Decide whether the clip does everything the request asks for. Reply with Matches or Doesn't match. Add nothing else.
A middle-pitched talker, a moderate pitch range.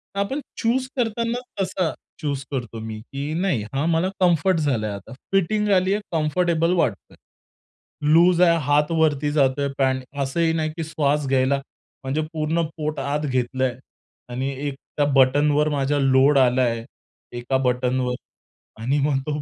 Matches